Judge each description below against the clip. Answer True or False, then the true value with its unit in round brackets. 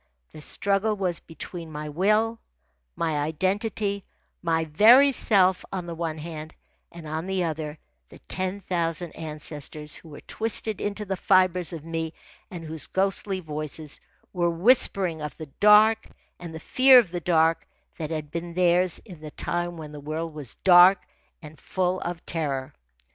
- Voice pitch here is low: False (170 Hz)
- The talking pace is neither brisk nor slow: True (160 wpm)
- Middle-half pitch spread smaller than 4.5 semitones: True (3.5 semitones)